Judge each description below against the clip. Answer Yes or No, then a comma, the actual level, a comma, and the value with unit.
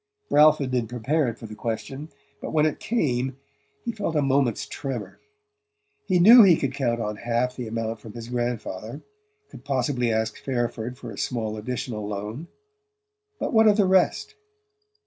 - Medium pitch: No, low, 125 Hz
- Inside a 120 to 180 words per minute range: Yes, average, 165 wpm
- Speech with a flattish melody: No, average, 4.6 semitones